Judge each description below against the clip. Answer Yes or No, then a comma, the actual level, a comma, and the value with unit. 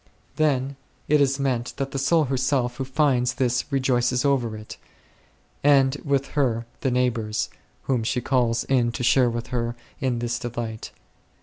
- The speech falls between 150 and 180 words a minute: Yes, average, 165 wpm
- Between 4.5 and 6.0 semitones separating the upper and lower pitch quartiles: No, narrow, 2.4 semitones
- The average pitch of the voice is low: Yes, low, 125 Hz